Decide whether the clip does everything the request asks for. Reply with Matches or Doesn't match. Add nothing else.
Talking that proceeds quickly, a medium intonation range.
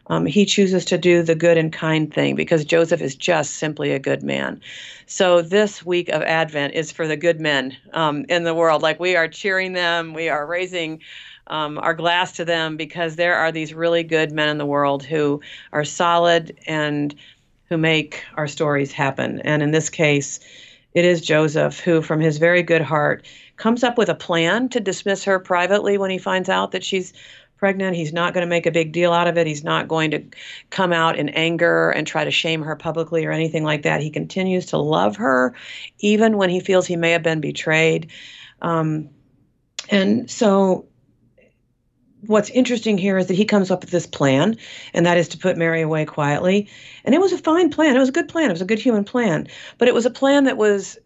Matches